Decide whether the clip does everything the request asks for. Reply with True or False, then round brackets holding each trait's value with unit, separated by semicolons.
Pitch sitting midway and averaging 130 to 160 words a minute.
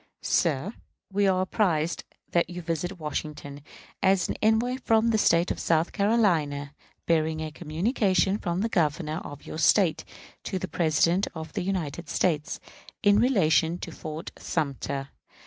True (170 Hz; 145 wpm)